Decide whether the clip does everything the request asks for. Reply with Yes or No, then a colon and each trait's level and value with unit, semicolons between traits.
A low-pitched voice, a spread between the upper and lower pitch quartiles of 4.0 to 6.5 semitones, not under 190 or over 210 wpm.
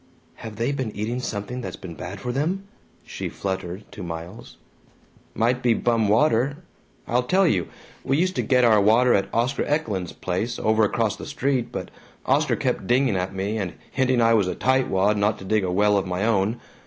Yes: low, 110 Hz; average, 4.3 semitones; average, 195 wpm